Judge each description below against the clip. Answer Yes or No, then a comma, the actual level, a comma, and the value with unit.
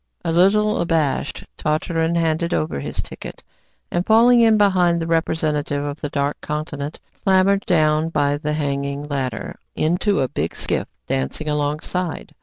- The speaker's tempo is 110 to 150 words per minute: Yes, average, 145 wpm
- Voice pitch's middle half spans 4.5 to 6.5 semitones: No, average, 3.5 semitones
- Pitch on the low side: No, medium, 155 Hz